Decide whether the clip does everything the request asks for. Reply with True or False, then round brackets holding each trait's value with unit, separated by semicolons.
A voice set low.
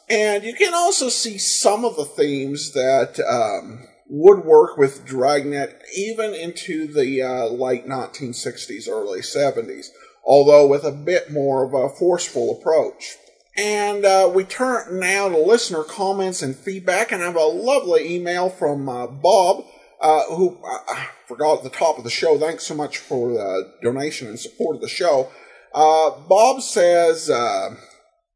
False (185 Hz)